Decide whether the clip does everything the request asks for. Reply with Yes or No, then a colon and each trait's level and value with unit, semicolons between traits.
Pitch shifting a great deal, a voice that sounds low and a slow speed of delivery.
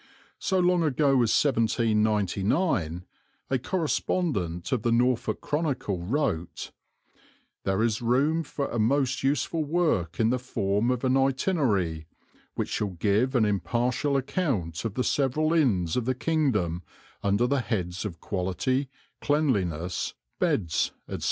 Yes: wide, 6.4 semitones; low, 120 Hz; slow, 130 wpm